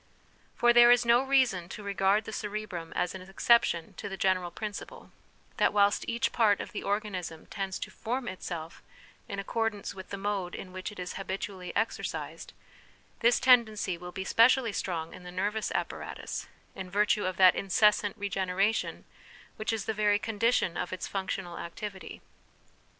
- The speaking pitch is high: Yes, high, 200 Hz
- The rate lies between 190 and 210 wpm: No, average, 165 wpm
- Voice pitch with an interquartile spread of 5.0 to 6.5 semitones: No, average, 2.9 semitones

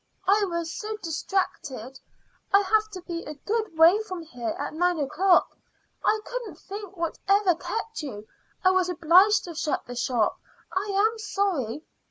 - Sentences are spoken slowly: No, average, 160 wpm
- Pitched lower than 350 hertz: No, very high, 360 Hz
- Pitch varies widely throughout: No, average, 4.4 semitones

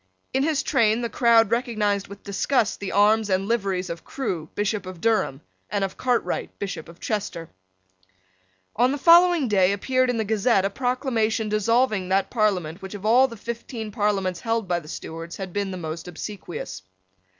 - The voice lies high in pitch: Yes, high, 210 Hz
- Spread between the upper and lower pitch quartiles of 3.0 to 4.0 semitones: Yes, average, 3.7 semitones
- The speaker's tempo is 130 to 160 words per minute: No, average, 175 wpm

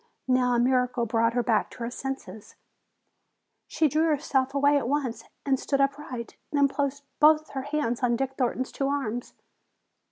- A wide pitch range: No, narrow, 2.6 semitones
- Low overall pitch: No, very high, 265 Hz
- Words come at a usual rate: Yes, average, 165 wpm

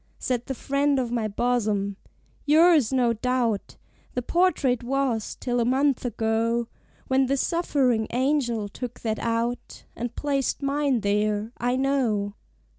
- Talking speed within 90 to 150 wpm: Yes, slow, 135 wpm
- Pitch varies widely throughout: No, average, 3.2 semitones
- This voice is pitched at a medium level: No, high, 245 Hz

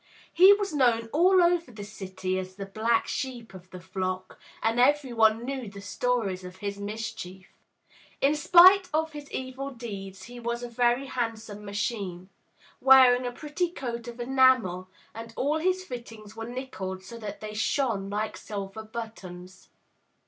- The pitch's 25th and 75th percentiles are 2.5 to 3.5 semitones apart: No, average, 4.8 semitones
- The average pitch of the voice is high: Yes, high, 230 Hz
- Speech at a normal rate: Yes, average, 160 wpm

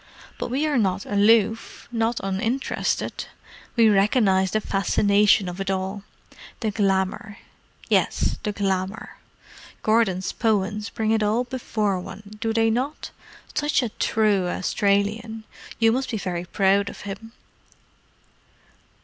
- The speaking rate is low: Yes, slow, 120 wpm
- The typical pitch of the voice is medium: No, high, 210 Hz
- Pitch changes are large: No, narrow, 2.5 semitones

